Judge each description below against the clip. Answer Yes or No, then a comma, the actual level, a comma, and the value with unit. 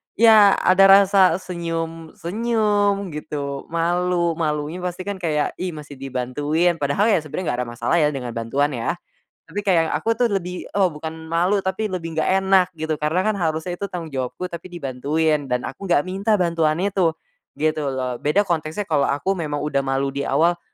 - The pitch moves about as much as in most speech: Yes, average, 4.2 semitones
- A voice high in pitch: No, medium, 165 Hz